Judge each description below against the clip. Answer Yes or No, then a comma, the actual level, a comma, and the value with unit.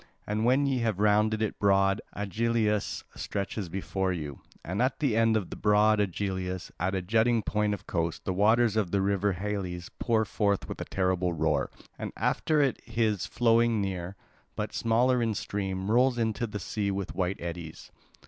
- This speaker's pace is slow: No, average, 175 wpm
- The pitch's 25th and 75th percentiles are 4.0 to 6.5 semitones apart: No, average, 3.2 semitones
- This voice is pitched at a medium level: No, low, 105 Hz